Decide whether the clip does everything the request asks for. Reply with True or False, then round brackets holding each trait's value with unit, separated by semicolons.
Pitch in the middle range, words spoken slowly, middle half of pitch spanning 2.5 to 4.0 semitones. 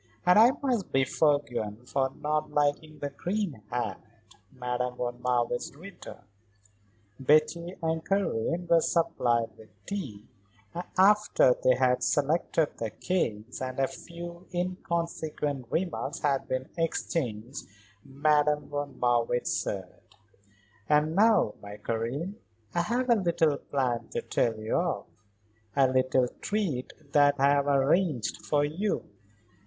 False (145 Hz; 125 wpm; 5.4 semitones)